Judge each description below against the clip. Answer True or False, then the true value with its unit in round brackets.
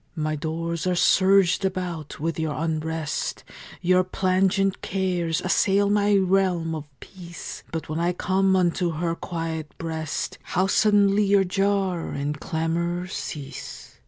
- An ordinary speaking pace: False (130 wpm)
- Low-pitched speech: False (175 Hz)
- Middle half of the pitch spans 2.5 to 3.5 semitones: True (2.9 semitones)